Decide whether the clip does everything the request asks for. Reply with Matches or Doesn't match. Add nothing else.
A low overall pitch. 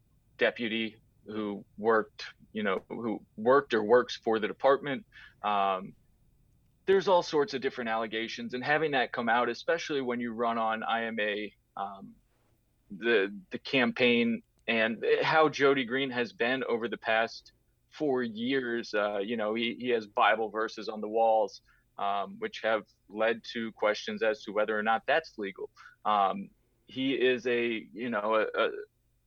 Matches